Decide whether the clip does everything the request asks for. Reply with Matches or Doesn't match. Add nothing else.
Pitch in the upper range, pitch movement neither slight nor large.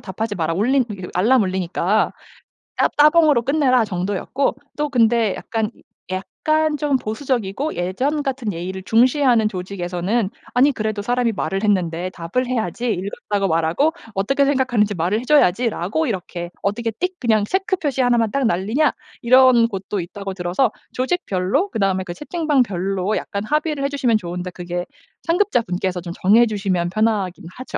Doesn't match